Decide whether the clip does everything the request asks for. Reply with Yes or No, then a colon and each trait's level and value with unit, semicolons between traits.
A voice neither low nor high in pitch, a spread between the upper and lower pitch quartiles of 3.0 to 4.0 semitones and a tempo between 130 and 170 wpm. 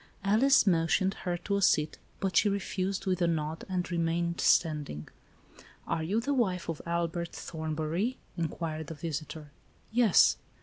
Yes: medium, 170 Hz; average, 3.4 semitones; average, 160 wpm